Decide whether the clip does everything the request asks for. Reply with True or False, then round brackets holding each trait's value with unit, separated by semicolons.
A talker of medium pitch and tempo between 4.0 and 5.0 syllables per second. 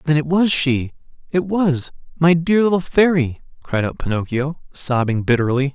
True (150 Hz; 4.7 syllables/s)